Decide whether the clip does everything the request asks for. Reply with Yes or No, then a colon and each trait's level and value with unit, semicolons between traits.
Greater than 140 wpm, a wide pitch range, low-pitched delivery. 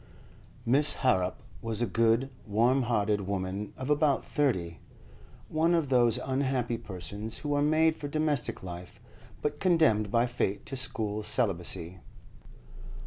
No: slow, 135 wpm; wide, 5.7 semitones; low, 120 Hz